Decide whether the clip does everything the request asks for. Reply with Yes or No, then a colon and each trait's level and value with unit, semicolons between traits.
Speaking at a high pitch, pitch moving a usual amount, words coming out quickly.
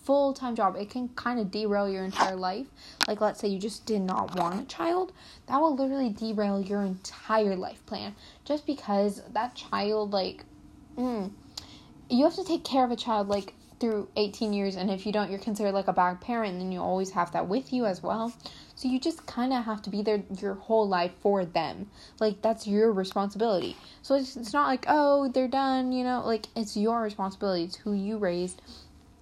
Yes: high, 215 Hz; average, 4.1 semitones; fast, 210 wpm